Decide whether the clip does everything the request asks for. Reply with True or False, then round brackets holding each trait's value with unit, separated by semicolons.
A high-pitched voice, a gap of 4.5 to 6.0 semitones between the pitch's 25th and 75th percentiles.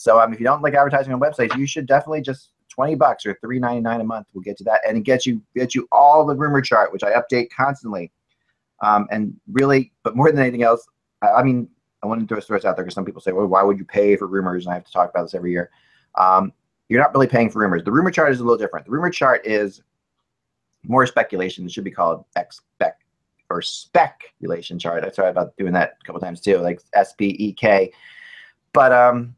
False (115 Hz; 5.0 semitones)